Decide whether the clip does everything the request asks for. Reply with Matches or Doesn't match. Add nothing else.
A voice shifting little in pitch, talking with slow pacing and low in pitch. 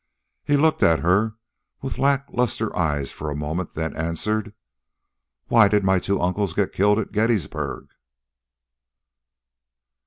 Doesn't match